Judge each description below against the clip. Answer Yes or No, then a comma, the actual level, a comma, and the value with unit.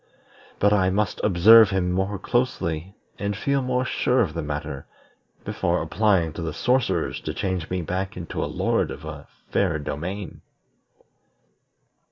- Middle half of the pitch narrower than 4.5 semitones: Yes, average, 3.9 semitones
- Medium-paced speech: Yes, average, 150 wpm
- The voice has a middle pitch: No, very low, 95 Hz